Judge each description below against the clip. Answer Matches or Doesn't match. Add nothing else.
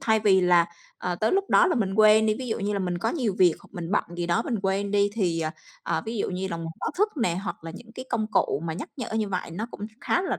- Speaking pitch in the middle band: Doesn't match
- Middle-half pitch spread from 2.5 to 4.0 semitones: Matches